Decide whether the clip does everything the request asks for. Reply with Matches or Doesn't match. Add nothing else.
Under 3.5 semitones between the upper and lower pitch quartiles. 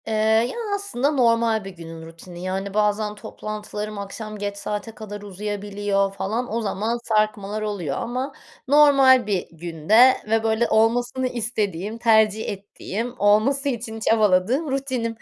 Matches